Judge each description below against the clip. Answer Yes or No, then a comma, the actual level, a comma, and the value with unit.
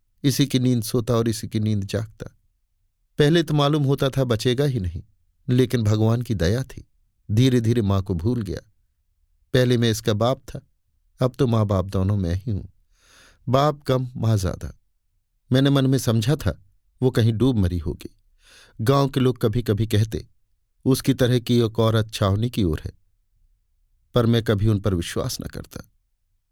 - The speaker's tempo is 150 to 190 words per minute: Yes, average, 175 wpm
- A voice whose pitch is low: Yes, low, 110 Hz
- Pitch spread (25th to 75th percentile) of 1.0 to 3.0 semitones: No, average, 4.7 semitones